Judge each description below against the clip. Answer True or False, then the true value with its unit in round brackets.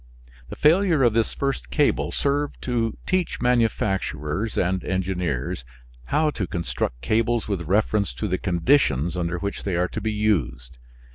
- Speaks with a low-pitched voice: True (105 Hz)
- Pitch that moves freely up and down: True (5.9 semitones)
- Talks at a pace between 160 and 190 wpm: False (150 wpm)